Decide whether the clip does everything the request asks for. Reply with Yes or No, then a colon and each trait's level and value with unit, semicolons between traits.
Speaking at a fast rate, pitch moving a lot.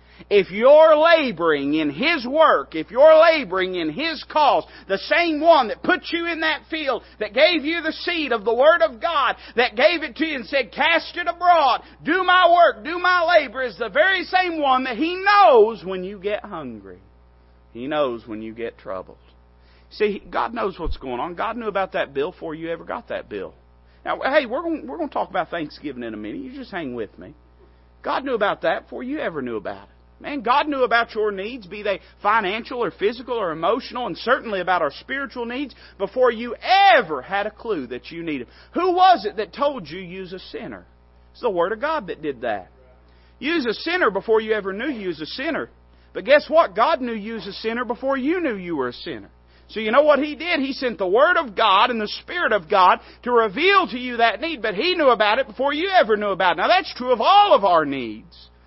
Yes: fast, 230 wpm; wide, 9.0 semitones